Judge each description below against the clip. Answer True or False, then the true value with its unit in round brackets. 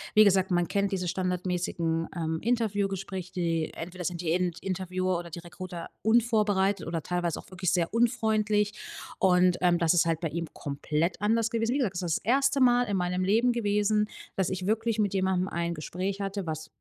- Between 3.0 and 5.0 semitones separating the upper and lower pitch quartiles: True (3.3 semitones)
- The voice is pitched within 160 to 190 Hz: True (185 Hz)